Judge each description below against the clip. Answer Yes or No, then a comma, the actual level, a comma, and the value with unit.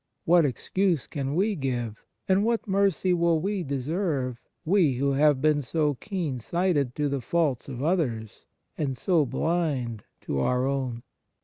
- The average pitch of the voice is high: No, medium, 145 Hz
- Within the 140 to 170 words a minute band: Yes, average, 150 wpm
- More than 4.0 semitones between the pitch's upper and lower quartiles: Yes, average, 5.2 semitones